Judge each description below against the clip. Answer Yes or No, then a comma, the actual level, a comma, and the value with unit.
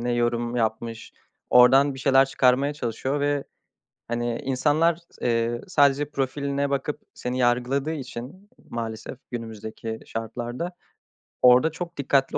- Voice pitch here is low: Yes, low, 130 Hz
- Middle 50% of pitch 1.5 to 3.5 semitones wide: Yes, average, 3.1 semitones